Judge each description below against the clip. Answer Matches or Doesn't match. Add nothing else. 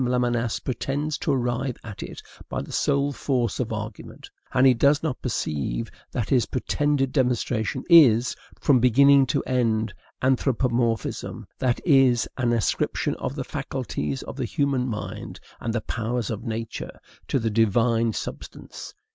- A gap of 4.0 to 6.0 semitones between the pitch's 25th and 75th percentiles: Doesn't match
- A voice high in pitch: Doesn't match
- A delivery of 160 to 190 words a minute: Doesn't match